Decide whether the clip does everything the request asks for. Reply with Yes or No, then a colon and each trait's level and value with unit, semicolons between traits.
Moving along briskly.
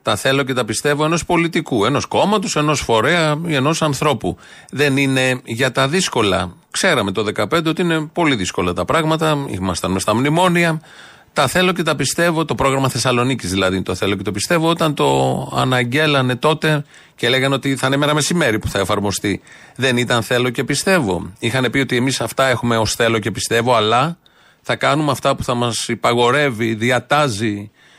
Yes: fast, 180 wpm